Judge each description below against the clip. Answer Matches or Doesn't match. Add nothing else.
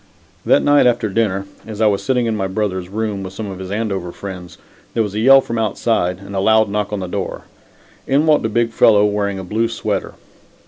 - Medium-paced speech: Doesn't match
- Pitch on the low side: Matches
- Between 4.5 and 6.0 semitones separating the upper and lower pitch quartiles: Doesn't match